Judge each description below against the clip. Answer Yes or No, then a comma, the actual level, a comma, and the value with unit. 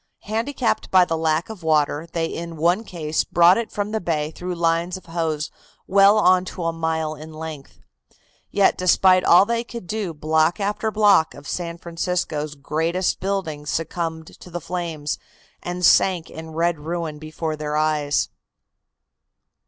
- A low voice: No, medium, 170 Hz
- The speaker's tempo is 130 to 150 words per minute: No, average, 160 wpm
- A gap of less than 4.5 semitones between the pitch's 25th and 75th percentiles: Yes, average, 2.8 semitones